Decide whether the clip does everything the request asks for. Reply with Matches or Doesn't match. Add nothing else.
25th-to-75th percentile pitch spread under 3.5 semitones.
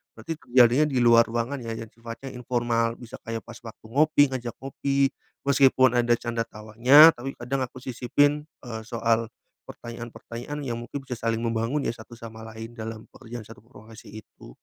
Matches